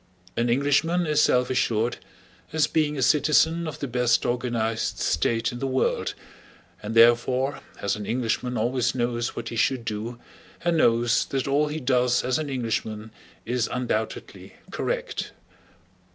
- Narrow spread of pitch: No, average, 3.0 semitones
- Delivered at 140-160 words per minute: Yes, average, 150 wpm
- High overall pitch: No, low, 125 Hz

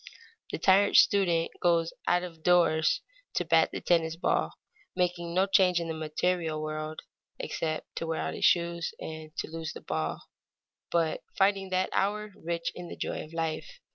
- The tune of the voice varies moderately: No, narrow, 2.1 semitones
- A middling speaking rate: Yes, average, 170 wpm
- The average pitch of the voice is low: No, medium, 170 Hz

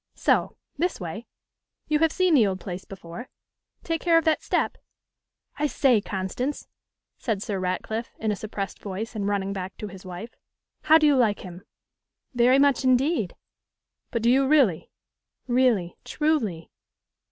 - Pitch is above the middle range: Yes, high, 225 Hz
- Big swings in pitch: Yes, wide, 6.4 semitones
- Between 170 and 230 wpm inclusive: No, average, 155 wpm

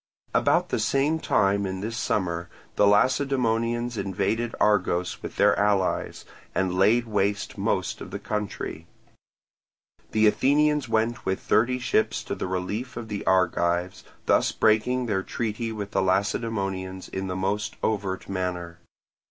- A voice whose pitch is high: No, low, 105 Hz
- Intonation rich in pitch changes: No, average, 3.6 semitones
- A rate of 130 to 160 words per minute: Yes, average, 140 wpm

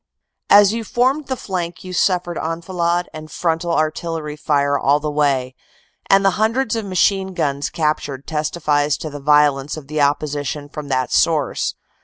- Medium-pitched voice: Yes, medium, 155 Hz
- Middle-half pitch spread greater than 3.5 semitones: Yes, average, 3.9 semitones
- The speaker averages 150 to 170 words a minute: Yes, average, 160 wpm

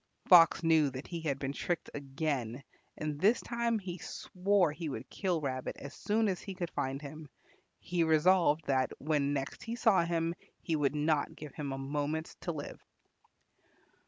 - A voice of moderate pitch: Yes, medium, 155 Hz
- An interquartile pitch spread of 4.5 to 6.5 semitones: No, average, 3.8 semitones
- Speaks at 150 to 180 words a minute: Yes, average, 175 wpm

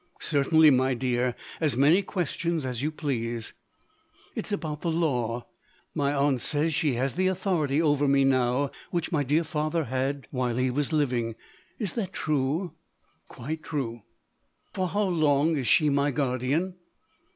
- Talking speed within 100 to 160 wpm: Yes, average, 150 wpm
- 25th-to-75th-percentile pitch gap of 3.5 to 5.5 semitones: Yes, average, 3.8 semitones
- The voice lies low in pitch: No, medium, 145 Hz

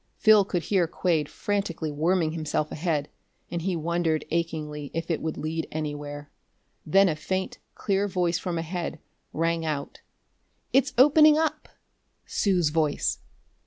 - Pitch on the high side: No, medium, 165 Hz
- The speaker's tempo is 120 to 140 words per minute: Yes, slow, 135 wpm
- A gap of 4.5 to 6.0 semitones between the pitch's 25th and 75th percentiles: No, average, 3.4 semitones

